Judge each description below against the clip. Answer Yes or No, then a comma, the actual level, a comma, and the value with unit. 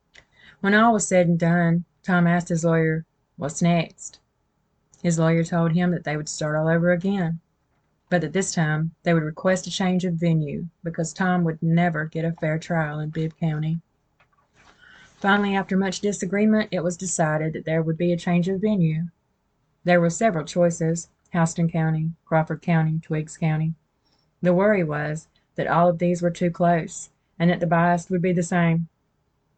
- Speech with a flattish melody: Yes, narrow, 1.9 semitones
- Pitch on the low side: No, medium, 170 Hz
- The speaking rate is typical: Yes, average, 180 wpm